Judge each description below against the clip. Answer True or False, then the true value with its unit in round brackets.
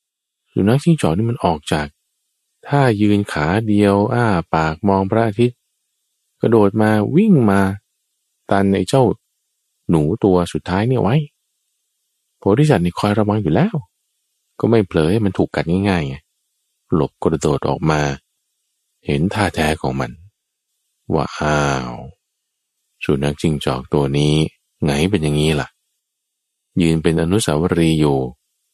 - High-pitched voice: False (95 Hz)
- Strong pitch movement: True (5.9 semitones)